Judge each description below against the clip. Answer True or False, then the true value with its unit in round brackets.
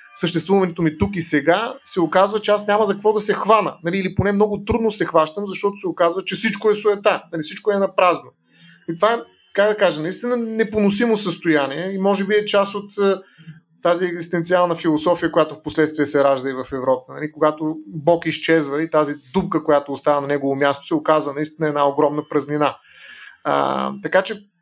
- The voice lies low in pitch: False (170 Hz)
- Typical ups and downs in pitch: True (4.7 semitones)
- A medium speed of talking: False (195 wpm)